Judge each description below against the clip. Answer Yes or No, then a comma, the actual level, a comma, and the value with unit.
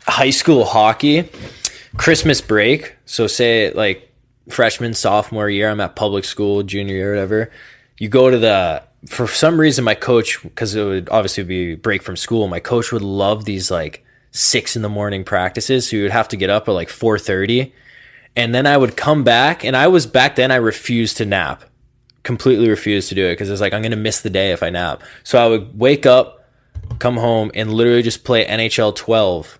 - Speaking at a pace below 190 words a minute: No, fast, 205 wpm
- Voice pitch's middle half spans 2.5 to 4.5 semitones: Yes, average, 3.5 semitones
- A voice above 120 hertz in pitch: No, low, 110 Hz